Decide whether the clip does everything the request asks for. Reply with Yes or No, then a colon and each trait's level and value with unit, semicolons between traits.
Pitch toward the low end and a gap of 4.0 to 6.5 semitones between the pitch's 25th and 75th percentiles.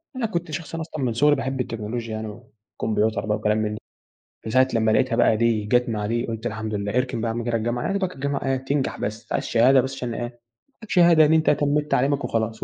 Yes: low, 120 Hz; average, 4.3 semitones